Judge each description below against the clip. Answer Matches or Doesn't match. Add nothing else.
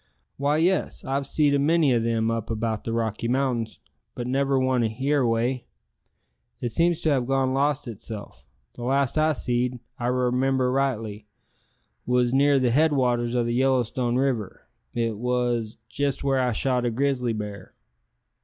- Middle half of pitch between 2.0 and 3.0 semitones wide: Matches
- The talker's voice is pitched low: Matches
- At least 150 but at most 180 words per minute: Matches